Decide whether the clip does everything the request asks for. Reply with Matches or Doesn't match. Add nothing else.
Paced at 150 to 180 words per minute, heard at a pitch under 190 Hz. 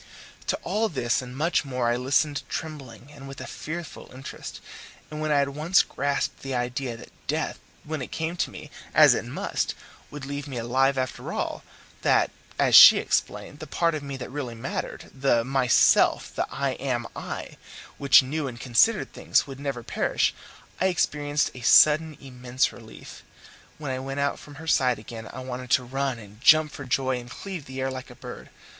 Doesn't match